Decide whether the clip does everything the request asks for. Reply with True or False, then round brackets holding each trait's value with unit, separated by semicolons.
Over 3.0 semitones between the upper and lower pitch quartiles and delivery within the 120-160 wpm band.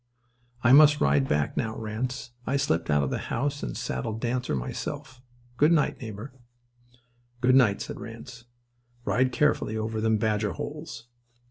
True (3.5 semitones; 150 wpm)